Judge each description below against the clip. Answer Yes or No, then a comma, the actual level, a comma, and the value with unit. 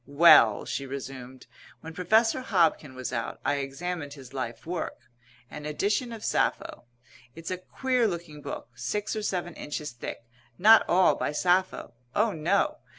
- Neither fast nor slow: Yes, average, 150 wpm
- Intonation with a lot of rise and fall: Yes, wide, 6.3 semitones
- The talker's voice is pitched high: No, medium, 165 Hz